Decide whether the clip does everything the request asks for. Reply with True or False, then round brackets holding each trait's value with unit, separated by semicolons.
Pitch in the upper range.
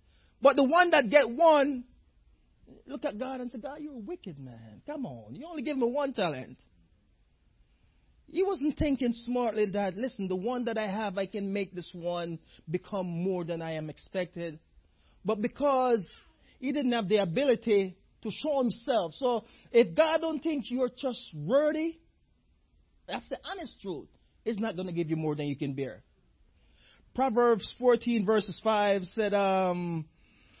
True (225 Hz)